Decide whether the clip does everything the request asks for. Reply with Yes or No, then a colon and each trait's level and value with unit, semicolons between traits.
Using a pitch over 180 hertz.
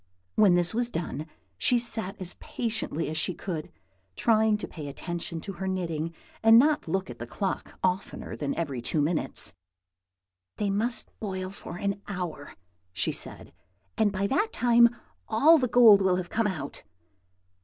Yes: high, 190 Hz